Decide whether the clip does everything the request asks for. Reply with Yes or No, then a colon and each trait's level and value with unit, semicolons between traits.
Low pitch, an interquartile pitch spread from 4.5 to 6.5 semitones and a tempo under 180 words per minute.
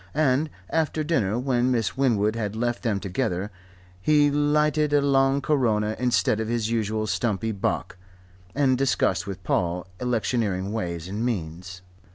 Yes: low, 115 Hz; average, 5.1 semitones; average, 145 wpm